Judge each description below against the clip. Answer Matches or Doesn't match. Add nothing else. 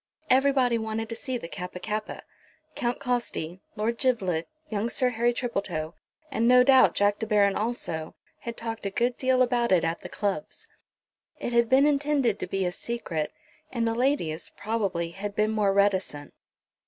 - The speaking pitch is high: Matches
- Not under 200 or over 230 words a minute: Doesn't match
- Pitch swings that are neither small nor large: Matches